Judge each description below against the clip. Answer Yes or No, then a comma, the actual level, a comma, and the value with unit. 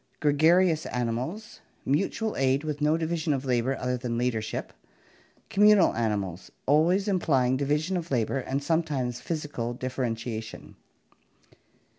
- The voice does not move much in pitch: No, average, 4.8 semitones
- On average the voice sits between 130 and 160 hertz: Yes, medium, 140 Hz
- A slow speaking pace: Yes, slow, 115 wpm